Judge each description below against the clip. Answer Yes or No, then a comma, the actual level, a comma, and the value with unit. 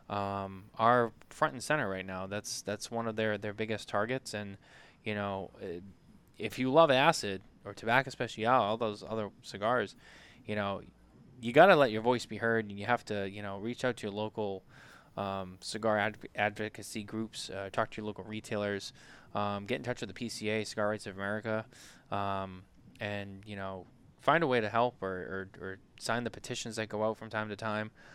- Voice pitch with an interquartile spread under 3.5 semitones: Yes, average, 2.7 semitones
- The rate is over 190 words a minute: Yes, average, 200 wpm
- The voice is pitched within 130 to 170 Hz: No, low, 105 Hz